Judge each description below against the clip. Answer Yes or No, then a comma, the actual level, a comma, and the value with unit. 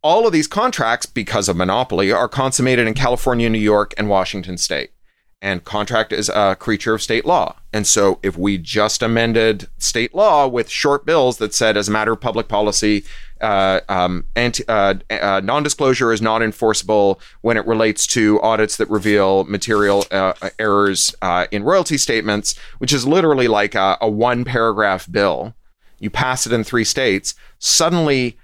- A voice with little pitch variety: No, average, 3.2 semitones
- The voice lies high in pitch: No, low, 110 Hz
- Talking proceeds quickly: No, average, 175 wpm